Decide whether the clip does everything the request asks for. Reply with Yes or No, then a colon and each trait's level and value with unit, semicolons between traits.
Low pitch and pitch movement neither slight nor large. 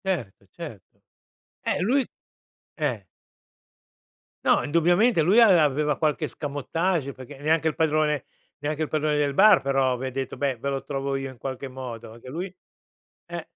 No: medium, 145 Hz; average, 3.4 semitones